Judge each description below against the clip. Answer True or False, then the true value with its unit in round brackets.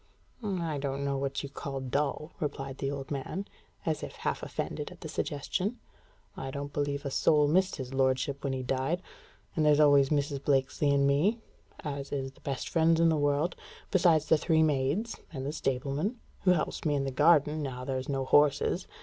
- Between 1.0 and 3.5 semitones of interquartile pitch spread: True (2.5 semitones)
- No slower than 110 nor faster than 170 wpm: False (190 wpm)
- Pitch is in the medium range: True (145 Hz)